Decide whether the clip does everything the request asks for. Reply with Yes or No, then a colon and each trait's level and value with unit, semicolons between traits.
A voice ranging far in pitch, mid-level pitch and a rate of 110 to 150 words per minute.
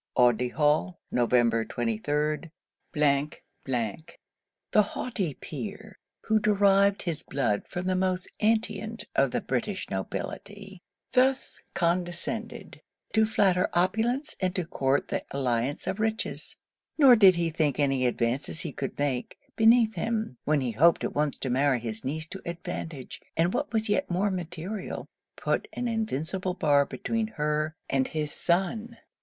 Yes: wide, 6.9 semitones; medium, 170 Hz; average, 140 wpm